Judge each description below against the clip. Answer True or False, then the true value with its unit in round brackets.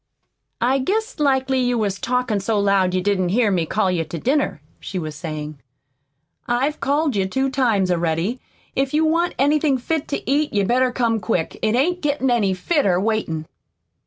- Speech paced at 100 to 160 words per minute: False (180 wpm)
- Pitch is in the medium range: False (235 Hz)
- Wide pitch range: True (6.4 semitones)